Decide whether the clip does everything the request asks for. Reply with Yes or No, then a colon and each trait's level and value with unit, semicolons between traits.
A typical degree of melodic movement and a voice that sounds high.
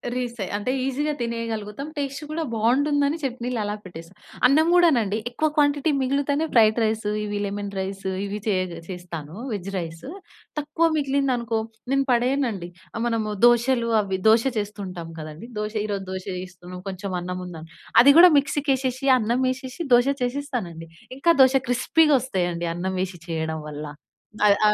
No: wide, 6.2 semitones; high, 225 Hz